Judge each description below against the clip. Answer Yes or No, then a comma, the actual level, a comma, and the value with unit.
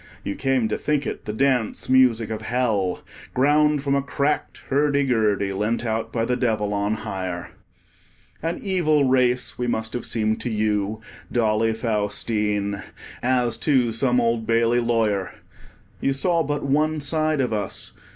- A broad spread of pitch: No, average, 4.1 semitones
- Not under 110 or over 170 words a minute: Yes, average, 155 wpm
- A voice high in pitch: No, low, 120 Hz